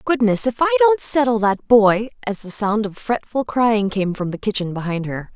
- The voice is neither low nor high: No, high, 220 Hz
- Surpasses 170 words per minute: Yes, average, 200 wpm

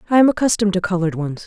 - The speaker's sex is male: No, female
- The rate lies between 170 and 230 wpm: No, fast, 245 wpm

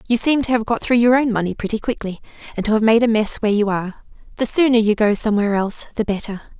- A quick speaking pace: Yes, fast, 255 wpm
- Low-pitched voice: No, high, 220 Hz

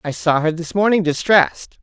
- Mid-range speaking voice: Yes, medium, 170 Hz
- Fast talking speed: No, average, 195 wpm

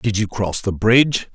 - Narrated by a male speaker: Yes, male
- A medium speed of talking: No, fast, 225 wpm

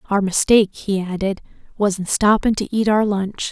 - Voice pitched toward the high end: Yes, high, 200 Hz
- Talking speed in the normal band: Yes, average, 190 wpm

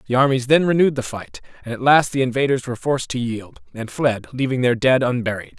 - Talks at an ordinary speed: No, fast, 225 wpm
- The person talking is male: Yes, male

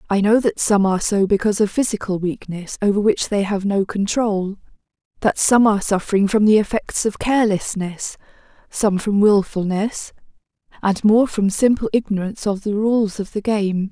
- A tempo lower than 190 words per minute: Yes, average, 170 wpm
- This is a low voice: No, high, 205 Hz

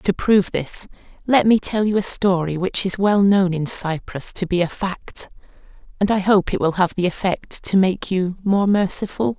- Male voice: No, female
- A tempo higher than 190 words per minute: Yes, fast, 205 wpm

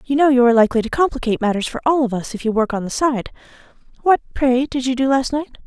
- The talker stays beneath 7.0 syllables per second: No, 7.1 syllables/s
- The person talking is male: No, female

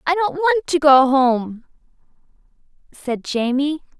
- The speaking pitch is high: Yes, very high, 290 Hz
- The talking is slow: Yes, slow, 120 wpm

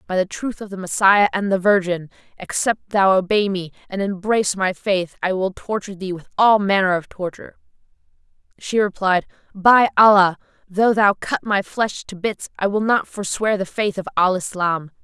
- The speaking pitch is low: No, high, 195 Hz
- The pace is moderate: Yes, average, 185 wpm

